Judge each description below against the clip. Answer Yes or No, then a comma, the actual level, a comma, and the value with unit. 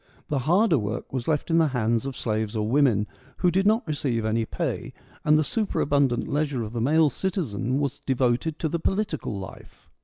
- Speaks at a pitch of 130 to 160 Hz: Yes, medium, 140 Hz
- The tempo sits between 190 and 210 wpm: Yes, average, 195 wpm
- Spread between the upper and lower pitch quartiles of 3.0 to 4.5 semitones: No, wide, 5.4 semitones